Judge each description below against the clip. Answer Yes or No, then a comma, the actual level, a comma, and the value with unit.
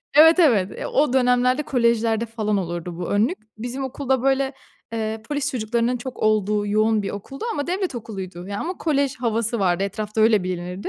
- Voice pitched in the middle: No, high, 230 Hz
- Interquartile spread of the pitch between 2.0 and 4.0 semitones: No, average, 4.4 semitones